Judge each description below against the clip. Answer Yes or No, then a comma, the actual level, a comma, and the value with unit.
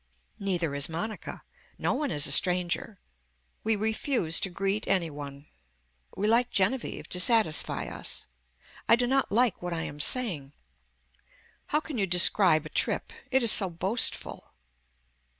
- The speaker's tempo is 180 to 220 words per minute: No, average, 150 wpm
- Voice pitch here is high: Yes, high, 195 Hz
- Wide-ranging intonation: Yes, wide, 5.7 semitones